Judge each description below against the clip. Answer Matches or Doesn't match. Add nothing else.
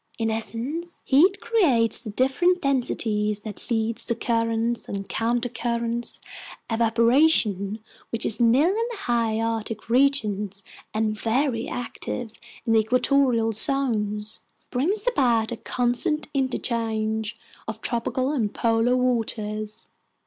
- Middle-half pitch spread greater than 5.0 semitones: Doesn't match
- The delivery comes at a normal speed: Doesn't match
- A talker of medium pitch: Doesn't match